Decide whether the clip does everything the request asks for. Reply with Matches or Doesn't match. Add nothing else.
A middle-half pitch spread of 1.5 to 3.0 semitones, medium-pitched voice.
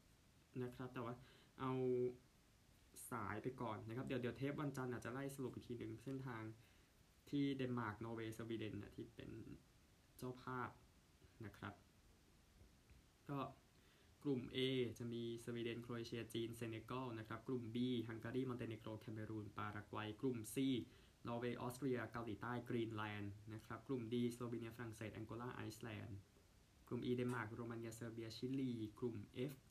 Doesn't match